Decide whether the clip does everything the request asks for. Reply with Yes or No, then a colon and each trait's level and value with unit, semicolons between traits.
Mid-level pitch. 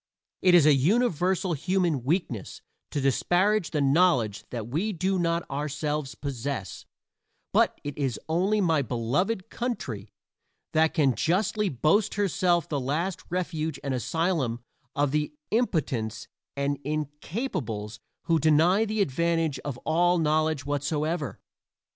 Yes: medium, 155 Hz